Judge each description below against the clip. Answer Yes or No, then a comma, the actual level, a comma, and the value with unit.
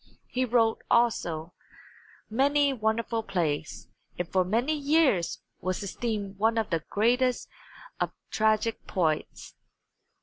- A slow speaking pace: Yes, slow, 110 wpm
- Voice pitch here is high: Yes, high, 220 Hz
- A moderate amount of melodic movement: Yes, average, 4.8 semitones